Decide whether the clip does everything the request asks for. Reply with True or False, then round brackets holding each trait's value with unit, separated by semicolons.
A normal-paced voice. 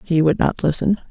False (215 wpm)